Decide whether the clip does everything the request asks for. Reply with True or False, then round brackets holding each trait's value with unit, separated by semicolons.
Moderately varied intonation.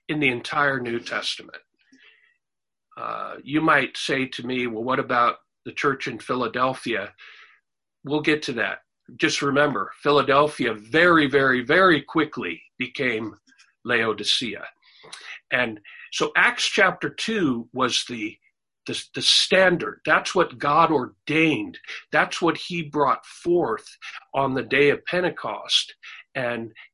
False (6.4 semitones)